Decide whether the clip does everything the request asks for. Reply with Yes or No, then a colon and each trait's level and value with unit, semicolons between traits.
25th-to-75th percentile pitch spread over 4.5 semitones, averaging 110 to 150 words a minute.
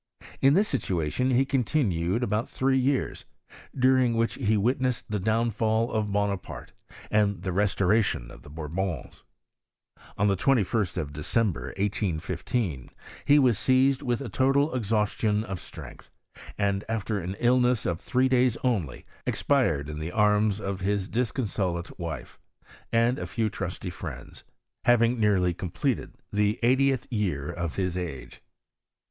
Yes: average, 5.1 semitones; average, 140 wpm